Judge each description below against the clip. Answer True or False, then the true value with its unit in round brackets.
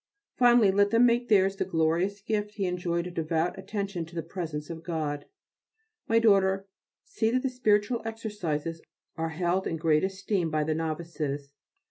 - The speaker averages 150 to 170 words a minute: True (165 wpm)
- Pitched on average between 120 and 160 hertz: False (185 Hz)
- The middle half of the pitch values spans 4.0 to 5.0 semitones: True (4.3 semitones)